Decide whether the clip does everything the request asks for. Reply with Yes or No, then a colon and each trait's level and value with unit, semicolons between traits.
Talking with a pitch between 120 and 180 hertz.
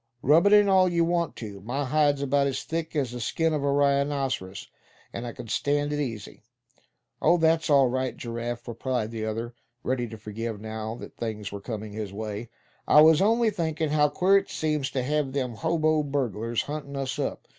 Yes: medium, 140 Hz